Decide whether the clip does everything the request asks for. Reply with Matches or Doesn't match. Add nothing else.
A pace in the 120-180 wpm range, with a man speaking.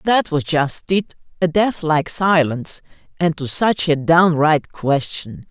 Doesn't match